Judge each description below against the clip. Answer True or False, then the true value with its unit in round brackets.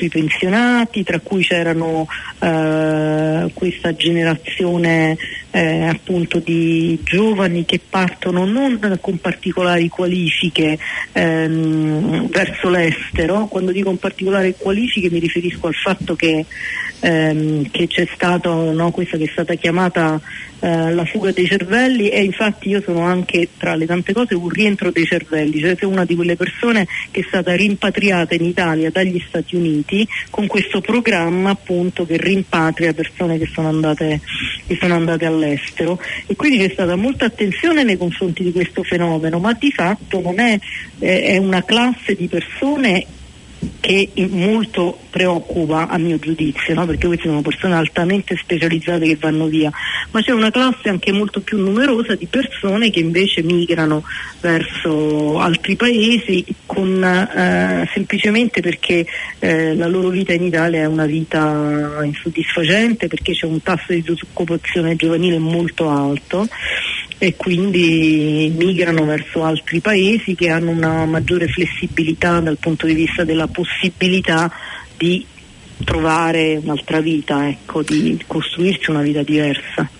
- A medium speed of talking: True (140 wpm)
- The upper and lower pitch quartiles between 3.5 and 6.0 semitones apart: False (2.9 semitones)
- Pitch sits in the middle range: True (175 Hz)